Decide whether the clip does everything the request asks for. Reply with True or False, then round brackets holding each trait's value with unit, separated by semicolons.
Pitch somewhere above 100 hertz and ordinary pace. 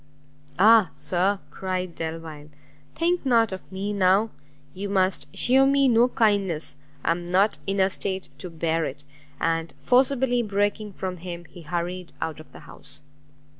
True (190 Hz; 155 wpm)